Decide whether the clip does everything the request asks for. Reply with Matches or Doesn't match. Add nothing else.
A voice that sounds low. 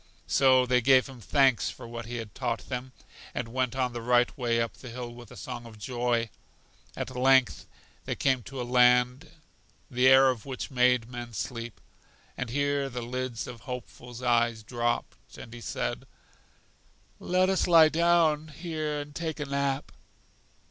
Matches